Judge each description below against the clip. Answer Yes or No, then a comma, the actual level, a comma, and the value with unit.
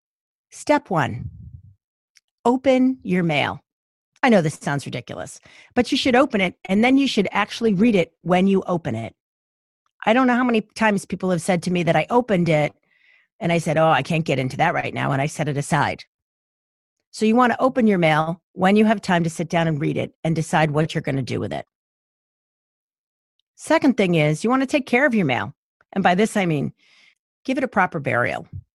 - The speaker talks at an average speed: No, fast, 215 wpm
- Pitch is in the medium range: Yes, medium, 180 Hz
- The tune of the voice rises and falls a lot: Yes, wide, 7.1 semitones